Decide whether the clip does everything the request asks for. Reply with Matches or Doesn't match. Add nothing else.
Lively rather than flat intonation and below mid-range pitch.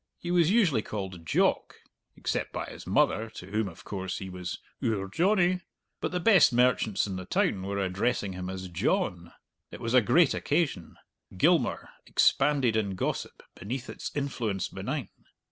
Matches